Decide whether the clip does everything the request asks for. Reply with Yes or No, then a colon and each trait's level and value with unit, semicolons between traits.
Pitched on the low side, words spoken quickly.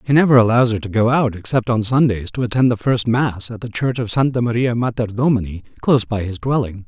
Yes: low, 115 Hz; fast, 235 wpm